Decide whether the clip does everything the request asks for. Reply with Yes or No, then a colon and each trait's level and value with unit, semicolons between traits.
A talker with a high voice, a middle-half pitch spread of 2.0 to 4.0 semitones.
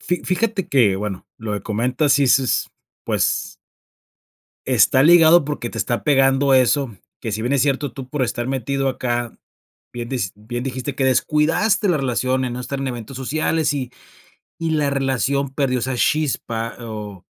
No: low, 130 Hz; average, 3.0 semitones